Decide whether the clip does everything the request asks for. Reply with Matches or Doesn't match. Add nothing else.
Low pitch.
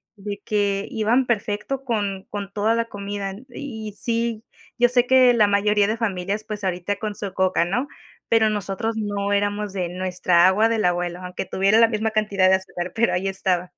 Doesn't match